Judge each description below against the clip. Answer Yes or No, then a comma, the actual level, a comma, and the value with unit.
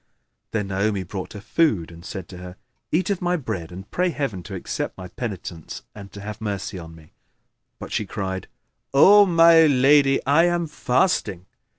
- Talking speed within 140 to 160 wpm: No, average, 180 wpm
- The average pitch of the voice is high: No, low, 105 Hz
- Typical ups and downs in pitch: No, wide, 8.5 semitones